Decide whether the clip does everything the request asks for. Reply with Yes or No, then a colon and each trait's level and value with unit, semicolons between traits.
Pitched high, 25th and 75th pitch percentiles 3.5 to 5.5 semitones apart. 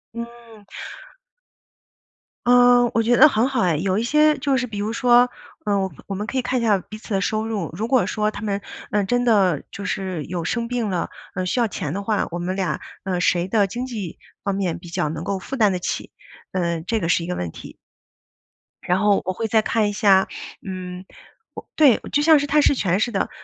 Yes: high, 210 Hz; average, 4.3 semitones